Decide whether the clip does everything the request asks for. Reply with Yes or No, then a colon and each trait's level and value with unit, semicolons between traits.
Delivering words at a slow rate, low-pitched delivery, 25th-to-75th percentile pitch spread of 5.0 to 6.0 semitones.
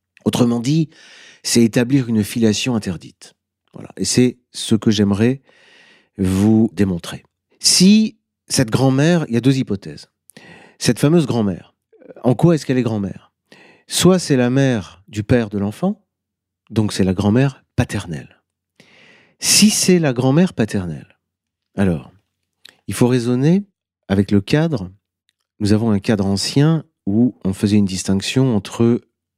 Yes: slow, 140 wpm; low, 115 Hz; wide, 5.4 semitones